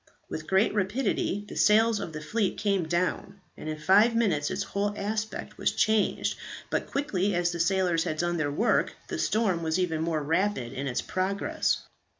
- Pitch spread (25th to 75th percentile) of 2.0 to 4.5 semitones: Yes, average, 4.1 semitones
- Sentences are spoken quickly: No, average, 180 wpm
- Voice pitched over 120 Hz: Yes, high, 190 Hz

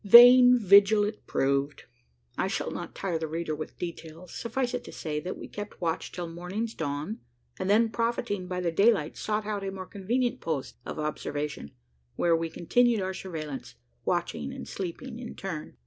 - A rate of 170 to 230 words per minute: Yes, average, 180 wpm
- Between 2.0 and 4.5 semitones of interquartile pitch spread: No, average, 5.2 semitones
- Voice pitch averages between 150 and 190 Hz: Yes, medium, 185 Hz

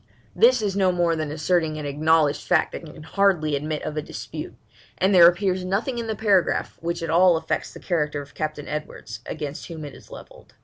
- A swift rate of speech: Yes, fast, 210 wpm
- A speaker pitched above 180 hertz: No, medium, 165 Hz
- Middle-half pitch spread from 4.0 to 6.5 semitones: No, average, 3.5 semitones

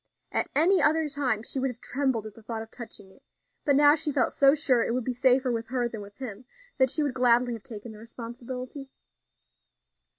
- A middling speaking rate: No, fast, 220 wpm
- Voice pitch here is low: No, very high, 250 Hz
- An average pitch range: Yes, average, 3.1 semitones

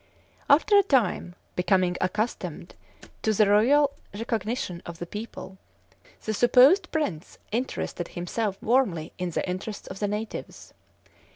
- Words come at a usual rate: No, slow, 125 wpm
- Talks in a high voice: Yes, high, 210 Hz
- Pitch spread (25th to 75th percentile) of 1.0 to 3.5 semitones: No, average, 5.2 semitones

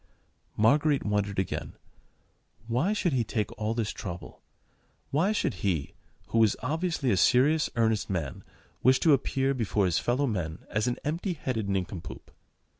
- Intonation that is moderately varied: No, wide, 6.1 semitones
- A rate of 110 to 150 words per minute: Yes, average, 140 wpm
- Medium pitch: No, low, 115 Hz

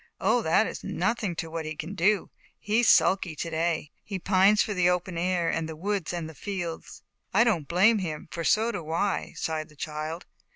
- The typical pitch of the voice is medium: Yes, medium, 175 Hz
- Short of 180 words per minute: No, average, 200 wpm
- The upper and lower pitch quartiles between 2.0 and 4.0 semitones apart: Yes, average, 3.7 semitones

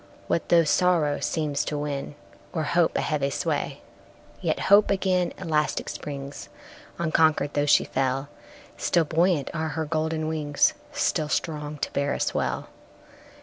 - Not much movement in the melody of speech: Yes, narrow, 2.2 semitones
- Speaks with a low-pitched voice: No, medium, 155 Hz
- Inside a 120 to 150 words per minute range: Yes, average, 145 wpm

